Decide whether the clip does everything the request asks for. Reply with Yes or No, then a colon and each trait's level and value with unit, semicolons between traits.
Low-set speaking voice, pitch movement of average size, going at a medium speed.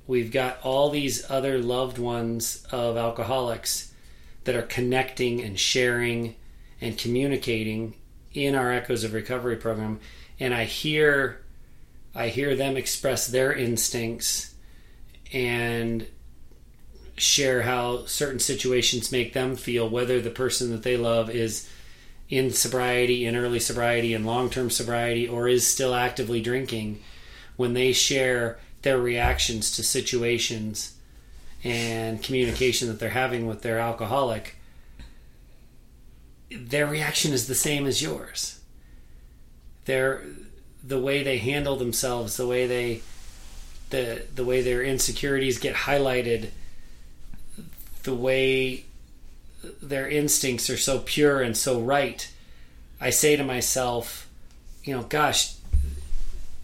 No: low, 120 Hz; average, 3.3 semitones; slow, 120 wpm